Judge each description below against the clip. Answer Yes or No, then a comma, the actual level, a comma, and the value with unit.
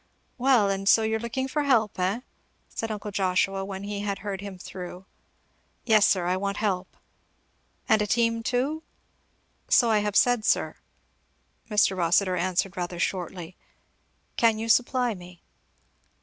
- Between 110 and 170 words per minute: Yes, average, 150 wpm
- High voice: Yes, high, 205 Hz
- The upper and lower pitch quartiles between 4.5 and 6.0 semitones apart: No, average, 3.3 semitones